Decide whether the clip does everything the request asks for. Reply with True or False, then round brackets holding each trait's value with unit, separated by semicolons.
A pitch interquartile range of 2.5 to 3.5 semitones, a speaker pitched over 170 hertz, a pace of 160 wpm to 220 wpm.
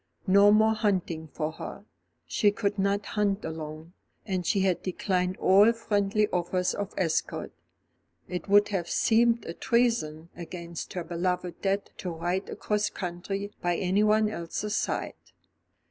False (3.1 semitones; 190 Hz; 140 wpm)